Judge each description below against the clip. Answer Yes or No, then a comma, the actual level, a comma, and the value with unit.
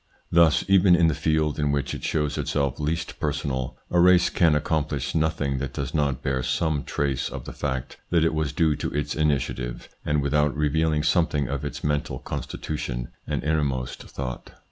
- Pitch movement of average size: No, narrow, 2.3 semitones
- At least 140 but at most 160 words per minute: No, average, 180 wpm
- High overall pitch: No, very low, 75 Hz